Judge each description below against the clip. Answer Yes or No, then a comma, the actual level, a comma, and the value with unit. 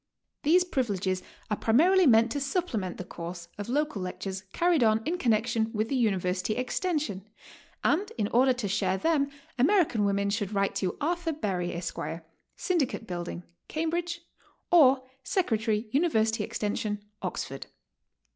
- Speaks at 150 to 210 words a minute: No, slow, 135 wpm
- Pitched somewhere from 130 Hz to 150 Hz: No, high, 225 Hz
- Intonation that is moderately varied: No, wide, 7.4 semitones